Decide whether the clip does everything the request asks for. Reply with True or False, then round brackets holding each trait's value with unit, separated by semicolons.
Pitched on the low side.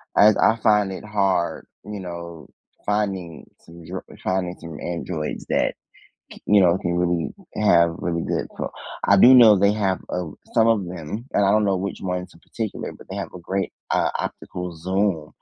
True (95 Hz)